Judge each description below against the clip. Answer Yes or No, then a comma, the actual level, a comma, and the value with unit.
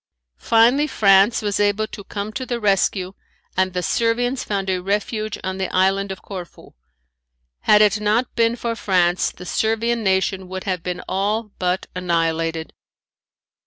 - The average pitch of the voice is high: Yes, high, 200 Hz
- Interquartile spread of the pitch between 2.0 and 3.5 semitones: Yes, average, 2.9 semitones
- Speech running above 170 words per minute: No, average, 155 wpm